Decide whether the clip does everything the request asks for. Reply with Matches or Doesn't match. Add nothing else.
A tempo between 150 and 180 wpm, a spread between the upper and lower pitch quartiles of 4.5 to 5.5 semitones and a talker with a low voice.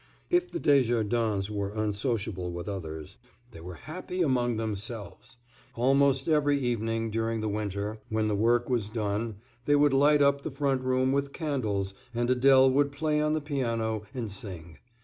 Matches